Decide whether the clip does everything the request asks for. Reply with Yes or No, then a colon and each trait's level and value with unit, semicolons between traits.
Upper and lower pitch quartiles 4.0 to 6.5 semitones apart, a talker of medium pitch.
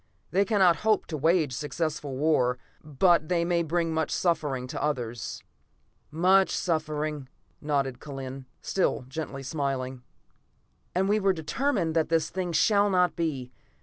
Yes: average, 4.4 semitones; medium, 155 Hz